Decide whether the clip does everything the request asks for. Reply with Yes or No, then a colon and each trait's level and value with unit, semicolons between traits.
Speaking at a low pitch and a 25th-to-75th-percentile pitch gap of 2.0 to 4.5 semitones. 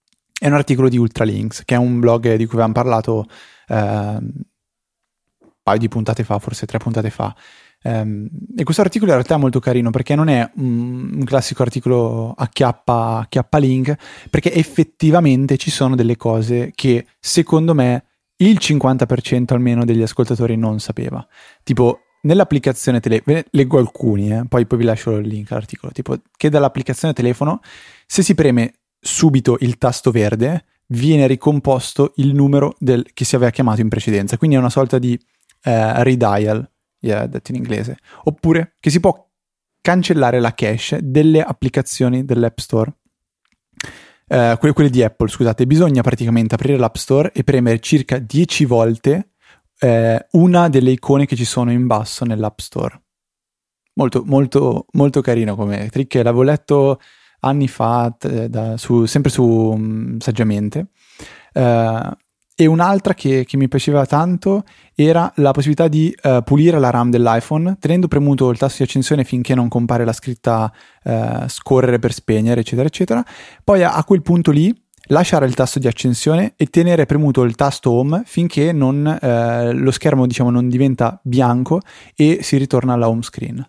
Yes: low, 130 Hz; average, 4.1 semitones